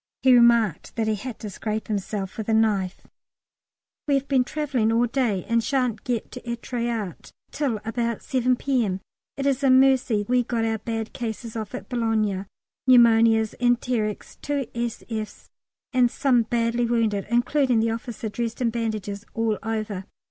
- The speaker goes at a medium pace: Yes, average, 160 wpm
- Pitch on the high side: Yes, high, 230 Hz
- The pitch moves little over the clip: Yes, narrow, 2.2 semitones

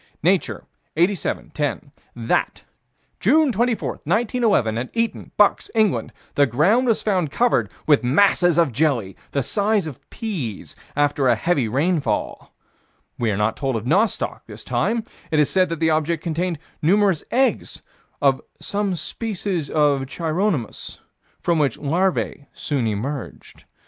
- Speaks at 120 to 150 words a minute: Yes, average, 140 wpm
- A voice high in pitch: No, medium, 160 Hz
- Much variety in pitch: Yes, wide, 6.7 semitones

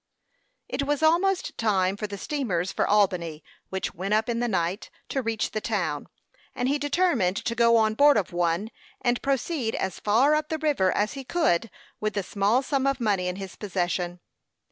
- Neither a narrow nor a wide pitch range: No, wide, 6.4 semitones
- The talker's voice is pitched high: Yes, high, 220 Hz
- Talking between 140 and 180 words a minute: No, average, 190 wpm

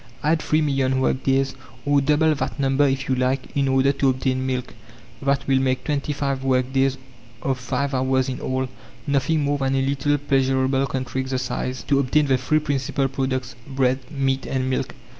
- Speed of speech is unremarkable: Yes, average, 185 wpm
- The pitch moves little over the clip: Yes, narrow, 1.2 semitones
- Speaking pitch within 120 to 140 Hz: Yes, low, 135 Hz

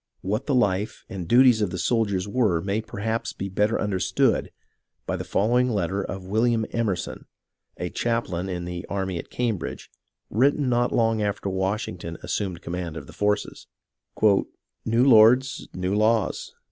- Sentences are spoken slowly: No, average, 160 wpm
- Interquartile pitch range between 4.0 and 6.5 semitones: No, average, 3.5 semitones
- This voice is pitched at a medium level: No, low, 105 Hz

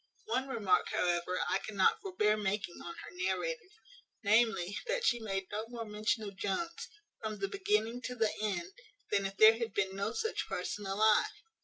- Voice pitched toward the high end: Yes, high, 215 Hz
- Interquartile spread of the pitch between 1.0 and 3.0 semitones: No, average, 5.1 semitones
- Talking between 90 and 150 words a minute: No, average, 175 wpm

